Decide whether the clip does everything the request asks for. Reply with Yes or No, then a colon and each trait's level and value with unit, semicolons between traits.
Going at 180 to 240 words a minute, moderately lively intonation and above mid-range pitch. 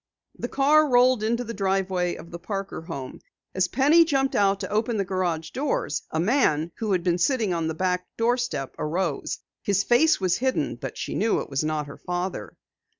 No: average, 195 wpm; wide, 6.1 semitones; high, 195 Hz